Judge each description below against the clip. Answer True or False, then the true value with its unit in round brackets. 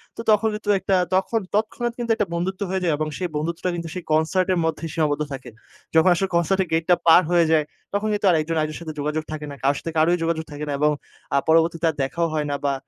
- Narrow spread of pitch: False (3.2 semitones)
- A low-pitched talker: False (165 Hz)